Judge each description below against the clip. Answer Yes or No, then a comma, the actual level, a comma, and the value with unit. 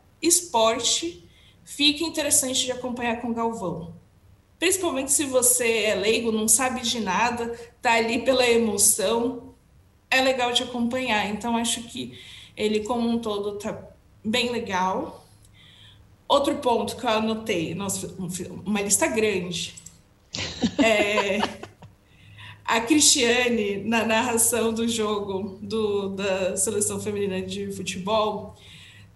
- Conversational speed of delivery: No, slow, 115 wpm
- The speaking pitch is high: Yes, high, 225 Hz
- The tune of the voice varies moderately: Yes, average, 3.7 semitones